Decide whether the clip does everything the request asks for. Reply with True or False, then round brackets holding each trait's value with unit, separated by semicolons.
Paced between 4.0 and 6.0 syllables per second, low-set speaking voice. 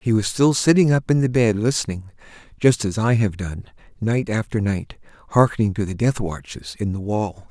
True (5.1 syllables/s; 110 Hz)